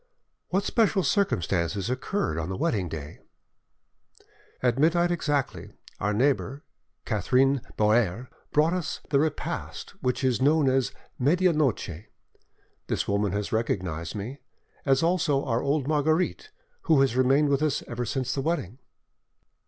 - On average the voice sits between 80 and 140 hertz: Yes, low, 135 Hz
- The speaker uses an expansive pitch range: Yes, wide, 6.3 semitones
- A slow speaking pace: Yes, slow, 130 wpm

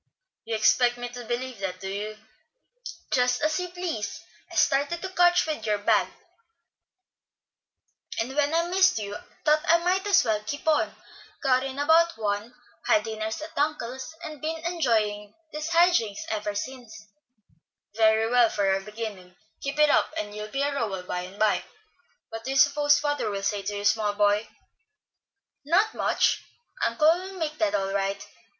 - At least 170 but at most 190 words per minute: Yes, average, 175 wpm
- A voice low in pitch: No, high, 245 Hz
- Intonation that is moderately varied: No, wide, 6.7 semitones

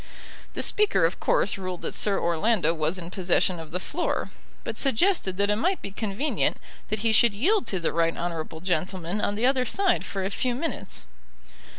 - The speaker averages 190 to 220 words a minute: Yes, average, 195 wpm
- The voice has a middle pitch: No, high, 200 Hz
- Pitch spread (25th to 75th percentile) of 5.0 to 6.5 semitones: Yes, average, 5.3 semitones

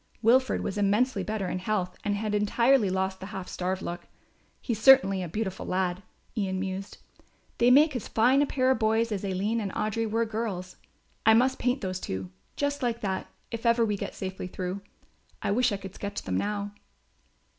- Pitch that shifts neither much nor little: Yes, average, 3.5 semitones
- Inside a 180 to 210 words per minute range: Yes, average, 190 wpm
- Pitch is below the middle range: No, high, 210 Hz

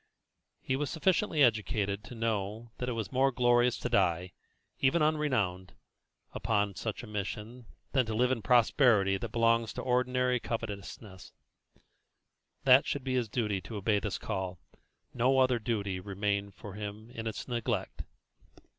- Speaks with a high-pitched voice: No, low, 115 Hz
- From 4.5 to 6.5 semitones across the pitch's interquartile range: No, average, 3.7 semitones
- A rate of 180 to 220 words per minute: No, average, 155 wpm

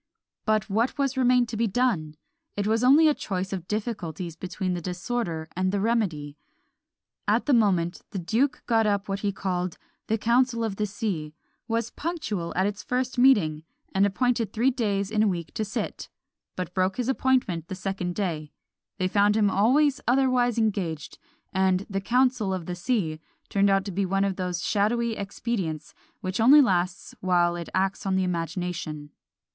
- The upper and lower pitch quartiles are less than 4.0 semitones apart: No, average, 4.4 semitones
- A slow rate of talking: No, average, 175 wpm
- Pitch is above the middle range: Yes, high, 200 Hz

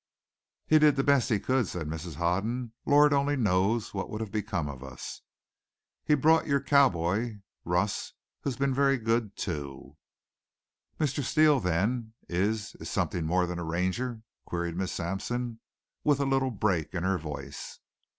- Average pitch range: No, wide, 7.2 semitones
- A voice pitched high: No, low, 110 Hz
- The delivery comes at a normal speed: Yes, average, 160 wpm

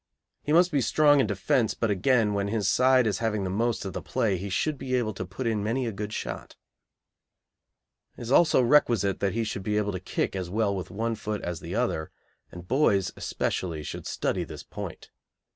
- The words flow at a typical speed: No, fast, 210 wpm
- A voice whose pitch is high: No, low, 110 Hz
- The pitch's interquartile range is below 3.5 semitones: No, average, 4.2 semitones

